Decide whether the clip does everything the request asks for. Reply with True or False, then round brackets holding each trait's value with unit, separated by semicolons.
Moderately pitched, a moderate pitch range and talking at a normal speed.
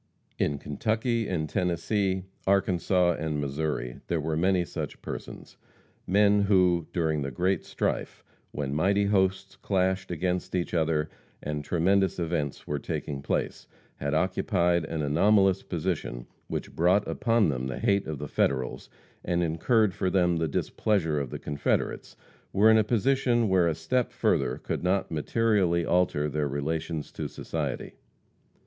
False (85 Hz; 4.1 semitones; 145 wpm)